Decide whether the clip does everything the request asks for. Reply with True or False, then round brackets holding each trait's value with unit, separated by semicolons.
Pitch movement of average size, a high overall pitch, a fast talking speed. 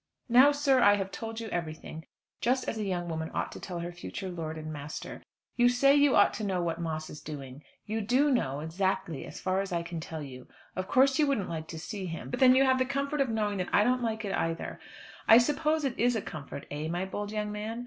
False (7.0 semitones; 200 Hz; 250 wpm)